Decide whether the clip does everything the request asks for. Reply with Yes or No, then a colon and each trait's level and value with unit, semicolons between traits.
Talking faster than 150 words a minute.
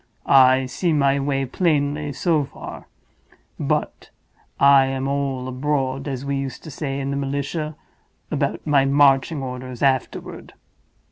No: slow, 135 wpm